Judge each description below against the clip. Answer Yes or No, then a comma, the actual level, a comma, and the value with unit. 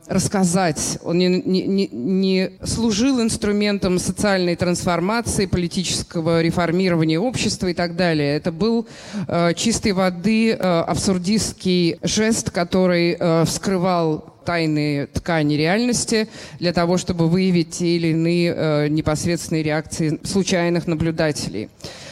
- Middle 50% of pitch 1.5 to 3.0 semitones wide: Yes, narrow, 2.5 semitones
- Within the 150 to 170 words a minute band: No, slow, 110 wpm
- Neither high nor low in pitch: Yes, medium, 175 Hz